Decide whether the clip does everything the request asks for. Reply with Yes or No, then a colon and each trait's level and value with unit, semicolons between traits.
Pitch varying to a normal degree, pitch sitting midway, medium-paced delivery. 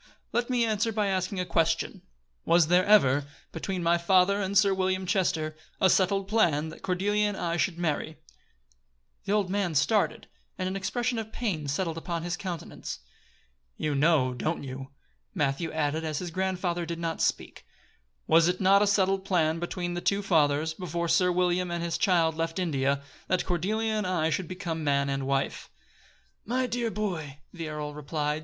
Yes: average, 3.2 semitones; medium, 175 Hz; average, 165 wpm